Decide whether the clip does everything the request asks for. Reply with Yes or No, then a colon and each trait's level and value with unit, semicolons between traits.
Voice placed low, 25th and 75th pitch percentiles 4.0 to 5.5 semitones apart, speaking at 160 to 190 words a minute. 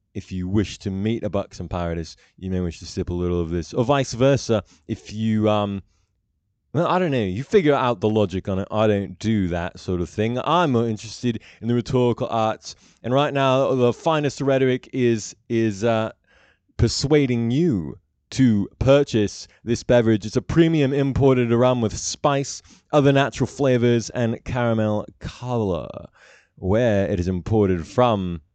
Yes: low, 115 Hz; average, 4.6 semitones; average, 170 wpm